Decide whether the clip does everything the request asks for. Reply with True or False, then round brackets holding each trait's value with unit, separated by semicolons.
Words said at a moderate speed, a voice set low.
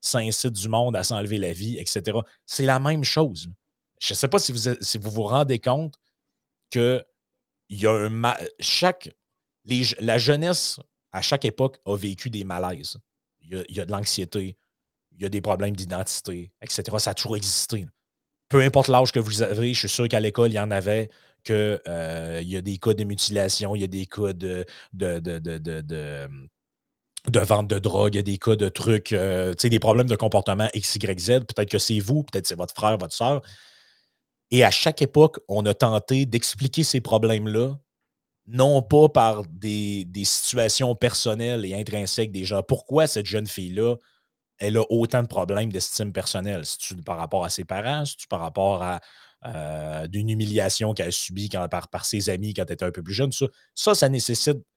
True (205 wpm; 105 Hz)